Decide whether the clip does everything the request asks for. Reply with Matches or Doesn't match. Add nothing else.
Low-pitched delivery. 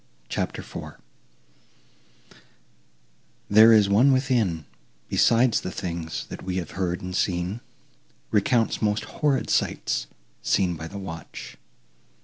Matches